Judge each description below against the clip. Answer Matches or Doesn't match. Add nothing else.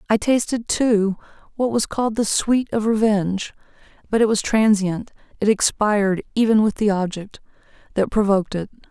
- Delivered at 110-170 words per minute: Matches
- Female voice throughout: Matches